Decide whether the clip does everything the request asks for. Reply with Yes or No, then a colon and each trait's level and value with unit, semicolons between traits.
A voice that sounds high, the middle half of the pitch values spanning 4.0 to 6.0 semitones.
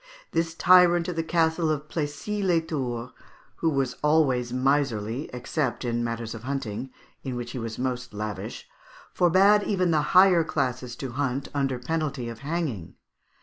No: medium, 140 Hz; average, 5.1 semitones